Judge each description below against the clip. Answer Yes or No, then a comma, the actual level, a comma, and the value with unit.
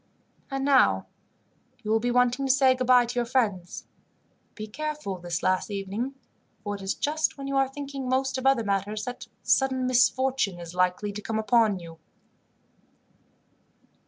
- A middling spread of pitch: Yes, average, 4.7 semitones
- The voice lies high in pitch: Yes, high, 245 Hz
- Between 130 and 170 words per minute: Yes, average, 160 wpm